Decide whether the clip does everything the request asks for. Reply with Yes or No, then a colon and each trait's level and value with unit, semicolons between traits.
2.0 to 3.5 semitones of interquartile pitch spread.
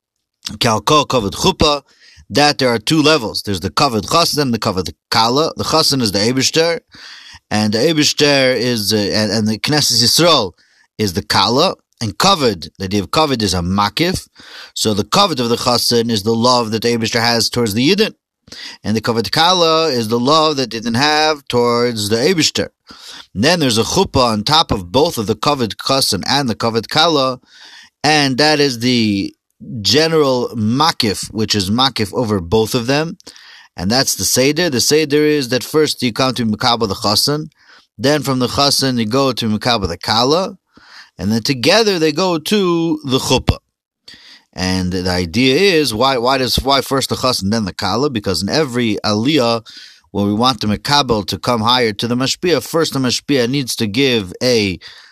No: average, 5.0 semitones